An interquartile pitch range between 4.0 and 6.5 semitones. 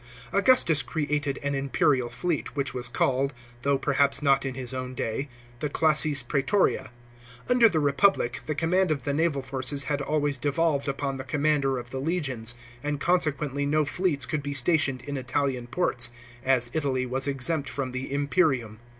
No: narrow, 2.6 semitones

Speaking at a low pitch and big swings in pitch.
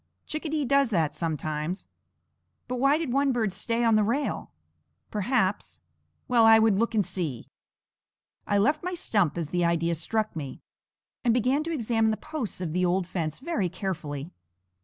No: high, 215 Hz; wide, 6.4 semitones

